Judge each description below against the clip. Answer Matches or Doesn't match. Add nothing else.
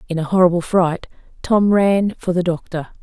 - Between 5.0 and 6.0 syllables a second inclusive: Matches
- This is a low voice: Doesn't match